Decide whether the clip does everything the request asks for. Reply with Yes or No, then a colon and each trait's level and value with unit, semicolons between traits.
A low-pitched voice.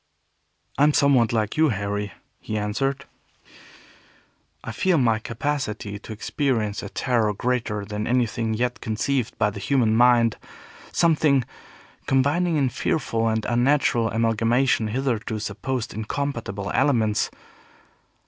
Yes: low, 115 Hz